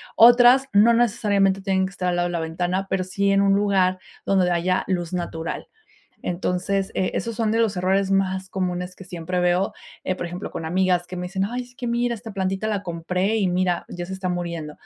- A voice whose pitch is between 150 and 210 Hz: Yes, high, 190 Hz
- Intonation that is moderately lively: No, narrow, 1.9 semitones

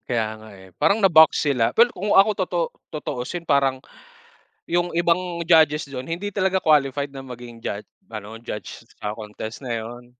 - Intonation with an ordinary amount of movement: No, wide, 6.5 semitones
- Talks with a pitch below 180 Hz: Yes, medium, 140 Hz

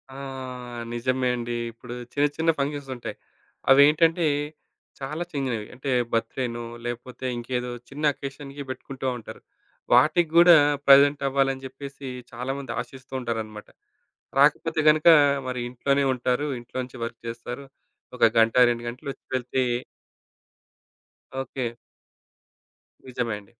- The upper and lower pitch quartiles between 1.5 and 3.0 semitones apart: Yes, narrow, 2.6 semitones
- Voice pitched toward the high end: No, low, 130 Hz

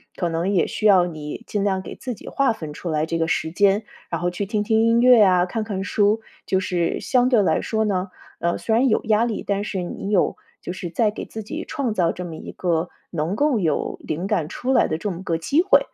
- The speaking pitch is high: Yes, high, 195 Hz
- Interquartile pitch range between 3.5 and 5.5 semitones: Yes, average, 4.2 semitones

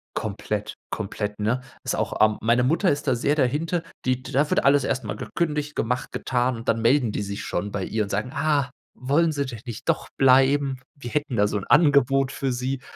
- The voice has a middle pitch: No, low, 130 Hz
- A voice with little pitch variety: No, average, 4.1 semitones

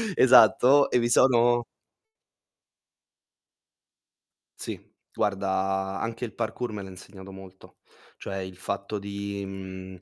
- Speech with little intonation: No, average, 3.4 semitones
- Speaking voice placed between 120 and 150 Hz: No, low, 100 Hz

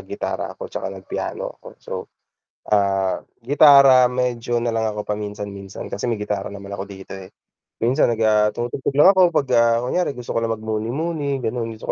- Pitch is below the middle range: Yes, low, 115 Hz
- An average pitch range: Yes, average, 3.7 semitones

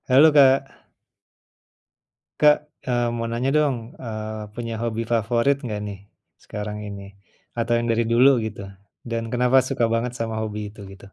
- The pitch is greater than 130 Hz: No, low, 115 Hz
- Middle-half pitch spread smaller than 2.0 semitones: No, narrow, 2.4 semitones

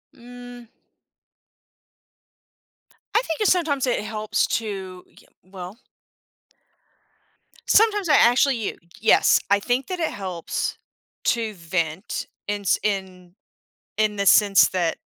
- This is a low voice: No, high, 210 Hz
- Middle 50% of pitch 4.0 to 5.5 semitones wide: Yes, average, 4.7 semitones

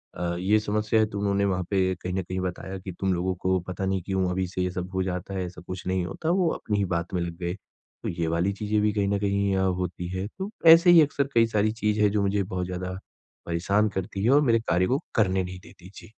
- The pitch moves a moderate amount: No, narrow, 2.2 semitones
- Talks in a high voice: No, very low, 95 Hz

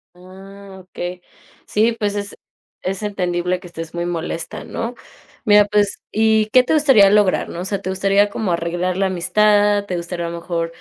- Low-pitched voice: No, high, 195 Hz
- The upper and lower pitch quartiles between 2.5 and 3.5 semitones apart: Yes, average, 2.8 semitones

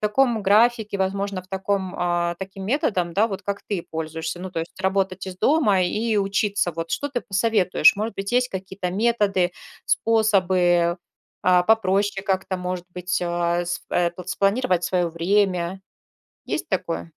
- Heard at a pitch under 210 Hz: Yes, high, 190 Hz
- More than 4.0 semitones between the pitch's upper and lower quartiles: No, narrow, 2.6 semitones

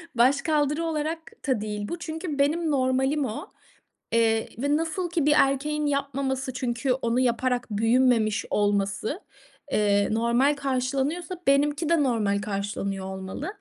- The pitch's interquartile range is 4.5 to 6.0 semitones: Yes, average, 4.8 semitones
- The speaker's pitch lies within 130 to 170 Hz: No, very high, 265 Hz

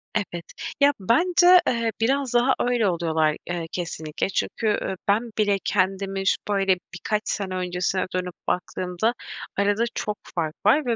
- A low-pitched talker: No, high, 200 Hz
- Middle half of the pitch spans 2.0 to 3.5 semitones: No, average, 4.3 semitones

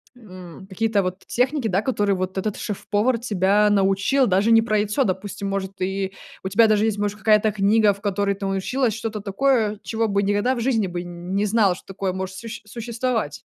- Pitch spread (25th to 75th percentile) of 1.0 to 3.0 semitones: Yes, narrow, 2.6 semitones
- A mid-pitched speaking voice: No, high, 205 Hz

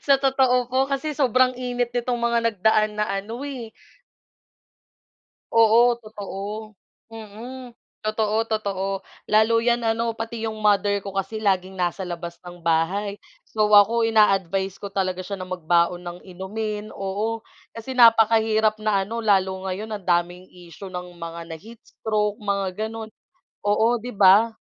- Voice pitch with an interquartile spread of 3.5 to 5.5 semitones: No, average, 3.0 semitones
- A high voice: Yes, high, 215 Hz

